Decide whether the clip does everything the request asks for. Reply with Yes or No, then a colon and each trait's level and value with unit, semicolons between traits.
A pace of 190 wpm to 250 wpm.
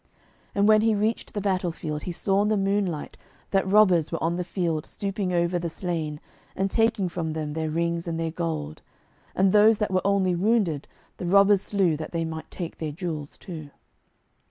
Yes: average, 195 wpm